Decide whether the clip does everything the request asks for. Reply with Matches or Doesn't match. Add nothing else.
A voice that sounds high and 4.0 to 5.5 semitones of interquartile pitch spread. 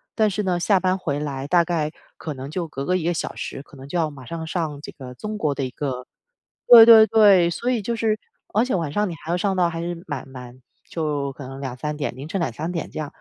Doesn't match